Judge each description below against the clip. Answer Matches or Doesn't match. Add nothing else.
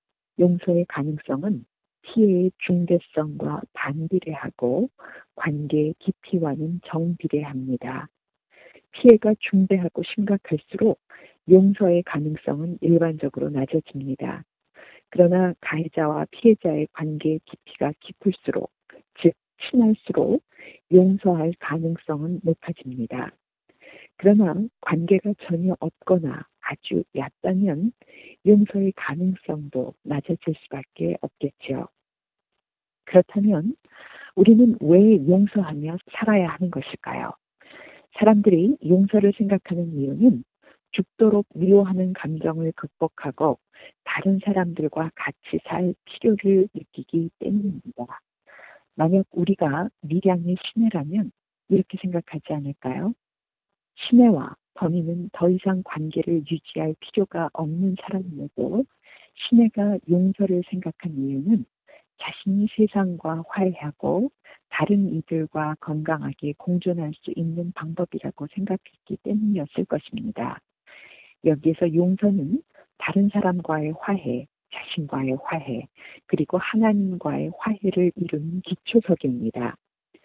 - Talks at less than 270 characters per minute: Matches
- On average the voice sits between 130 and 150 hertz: Doesn't match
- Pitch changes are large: Doesn't match